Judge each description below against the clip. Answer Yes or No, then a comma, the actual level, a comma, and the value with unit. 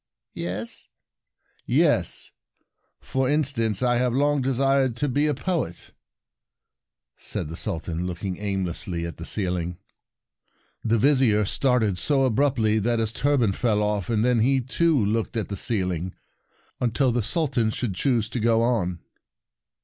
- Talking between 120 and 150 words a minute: Yes, average, 140 wpm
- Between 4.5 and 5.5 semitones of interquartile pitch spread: Yes, average, 4.9 semitones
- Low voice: Yes, low, 115 Hz